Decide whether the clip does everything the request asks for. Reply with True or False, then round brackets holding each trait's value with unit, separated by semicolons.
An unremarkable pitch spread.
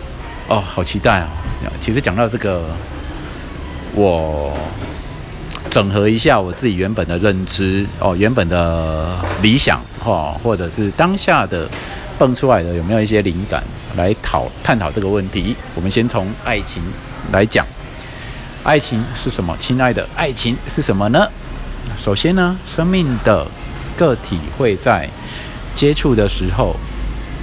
False (5.9 semitones)